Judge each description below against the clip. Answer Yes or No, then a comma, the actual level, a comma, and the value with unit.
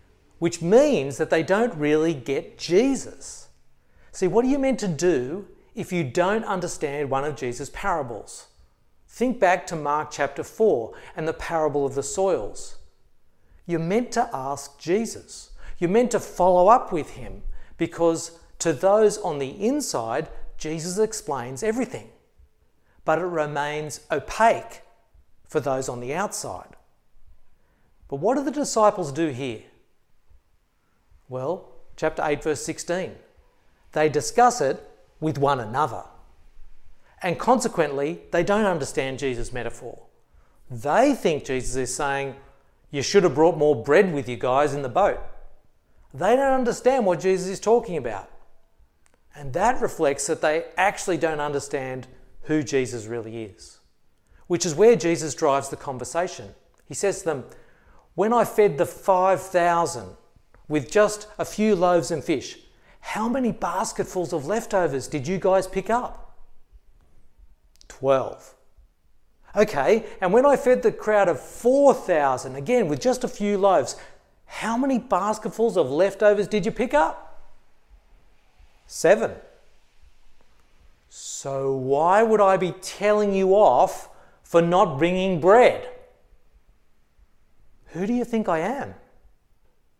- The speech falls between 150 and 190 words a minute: No, slow, 135 wpm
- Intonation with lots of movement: Yes, wide, 7.0 semitones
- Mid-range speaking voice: Yes, medium, 170 Hz